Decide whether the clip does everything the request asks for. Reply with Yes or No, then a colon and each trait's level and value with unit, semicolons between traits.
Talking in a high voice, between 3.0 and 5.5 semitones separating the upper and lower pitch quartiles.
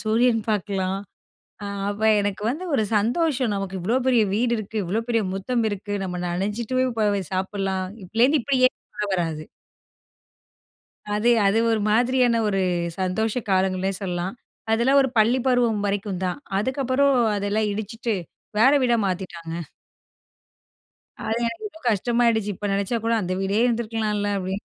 Yes: high, 215 Hz; average, 3.6 semitones